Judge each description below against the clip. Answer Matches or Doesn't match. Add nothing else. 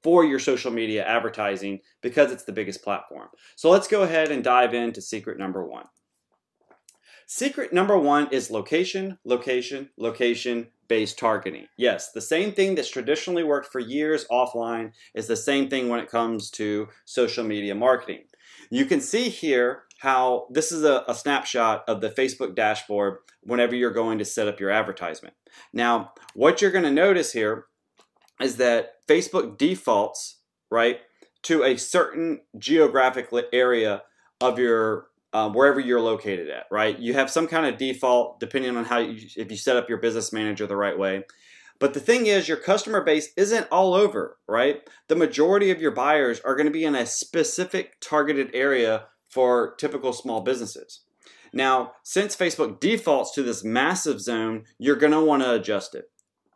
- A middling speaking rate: Matches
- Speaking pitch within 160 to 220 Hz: Doesn't match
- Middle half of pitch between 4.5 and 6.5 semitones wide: Matches